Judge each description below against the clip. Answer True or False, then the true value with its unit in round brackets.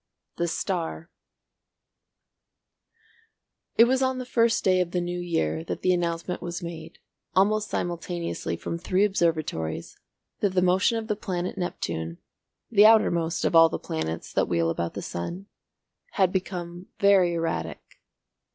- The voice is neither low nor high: True (175 Hz)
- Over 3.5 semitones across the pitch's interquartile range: False (2.8 semitones)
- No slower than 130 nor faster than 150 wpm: True (140 wpm)